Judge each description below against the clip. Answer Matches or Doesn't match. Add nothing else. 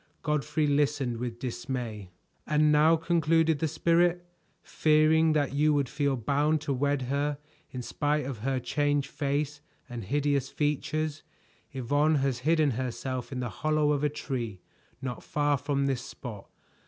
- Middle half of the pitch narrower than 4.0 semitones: Matches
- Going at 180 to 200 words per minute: Doesn't match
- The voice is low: Doesn't match